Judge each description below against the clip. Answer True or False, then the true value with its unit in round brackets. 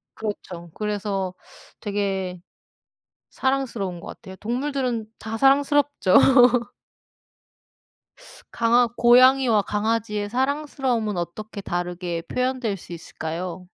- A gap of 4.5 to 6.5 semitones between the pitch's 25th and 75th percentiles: True (5.2 semitones)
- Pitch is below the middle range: False (215 Hz)